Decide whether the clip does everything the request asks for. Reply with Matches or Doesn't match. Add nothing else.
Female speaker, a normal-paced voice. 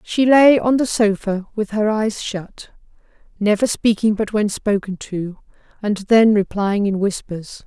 Matches